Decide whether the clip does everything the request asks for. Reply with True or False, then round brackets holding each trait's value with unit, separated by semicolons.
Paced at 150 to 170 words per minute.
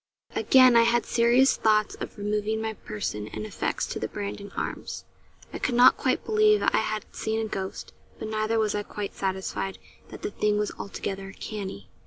False (185 wpm)